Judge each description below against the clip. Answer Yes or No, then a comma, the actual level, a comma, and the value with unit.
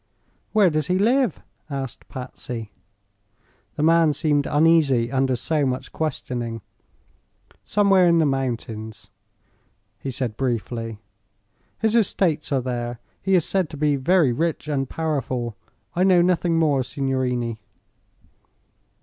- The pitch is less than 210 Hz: Yes, medium, 140 Hz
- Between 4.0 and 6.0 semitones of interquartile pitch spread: Yes, average, 5.0 semitones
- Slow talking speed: Yes, slow, 125 wpm